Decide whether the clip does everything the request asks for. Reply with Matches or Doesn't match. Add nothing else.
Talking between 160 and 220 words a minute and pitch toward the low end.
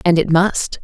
Doesn't match